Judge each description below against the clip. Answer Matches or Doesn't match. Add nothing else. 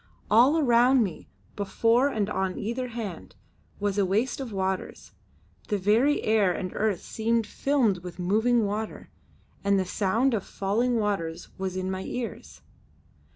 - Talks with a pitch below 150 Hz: Doesn't match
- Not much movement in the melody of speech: Doesn't match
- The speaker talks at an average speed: Matches